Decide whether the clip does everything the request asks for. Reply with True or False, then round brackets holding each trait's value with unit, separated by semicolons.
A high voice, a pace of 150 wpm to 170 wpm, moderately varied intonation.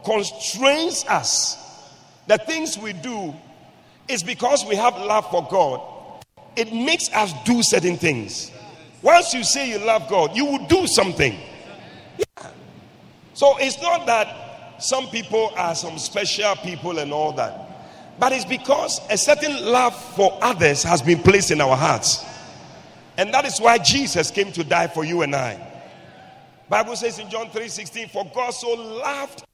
False (220 Hz; 160 wpm; 6.3 semitones)